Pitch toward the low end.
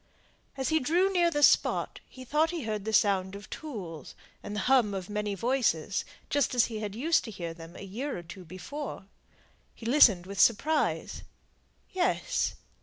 No: high, 220 Hz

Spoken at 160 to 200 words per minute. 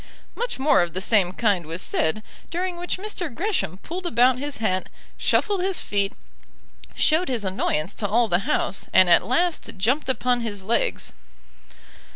Yes: average, 165 wpm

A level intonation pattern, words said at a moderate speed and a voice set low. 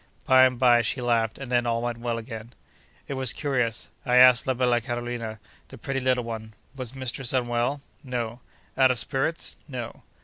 Yes: narrow, 1.8 semitones; average, 165 wpm; low, 120 Hz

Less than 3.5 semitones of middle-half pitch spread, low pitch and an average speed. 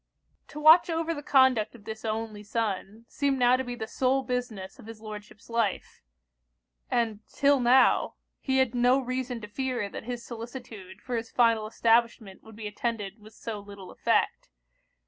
No: average, 3.0 semitones; high, 230 Hz; average, 170 wpm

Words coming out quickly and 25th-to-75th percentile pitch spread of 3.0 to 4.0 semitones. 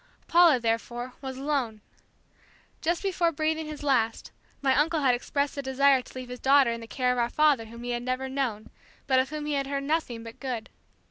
Yes: fast, 210 wpm; average, 3.3 semitones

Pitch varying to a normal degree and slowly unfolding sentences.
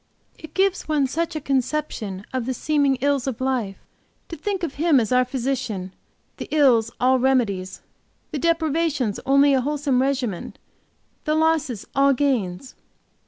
No: average, 3.6 semitones; average, 150 wpm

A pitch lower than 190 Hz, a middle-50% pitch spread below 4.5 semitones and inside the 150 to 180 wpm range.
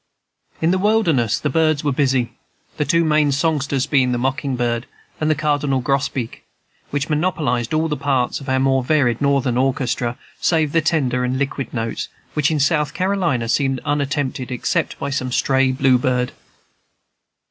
Yes: low, 135 Hz; average, 3.1 semitones; average, 165 wpm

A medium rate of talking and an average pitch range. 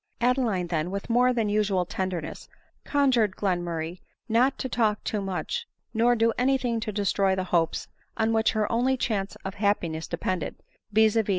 Yes: average, 175 wpm; average, 4.1 semitones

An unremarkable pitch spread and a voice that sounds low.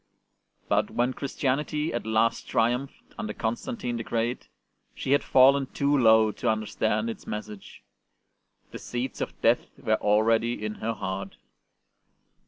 Yes: average, 3.1 semitones; low, 115 Hz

